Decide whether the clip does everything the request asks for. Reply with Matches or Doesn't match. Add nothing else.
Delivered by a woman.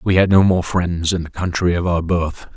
Doesn't match